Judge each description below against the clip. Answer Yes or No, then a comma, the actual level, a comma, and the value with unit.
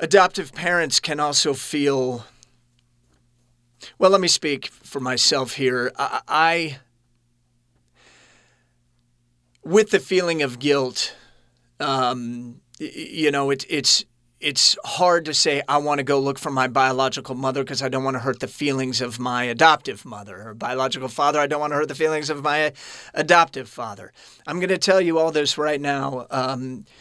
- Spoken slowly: No, average, 160 wpm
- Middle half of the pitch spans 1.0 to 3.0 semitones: No, average, 3.6 semitones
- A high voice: No, low, 135 Hz